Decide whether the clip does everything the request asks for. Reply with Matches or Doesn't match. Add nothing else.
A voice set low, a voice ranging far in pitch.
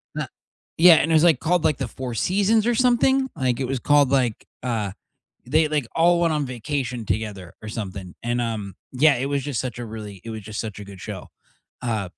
Matches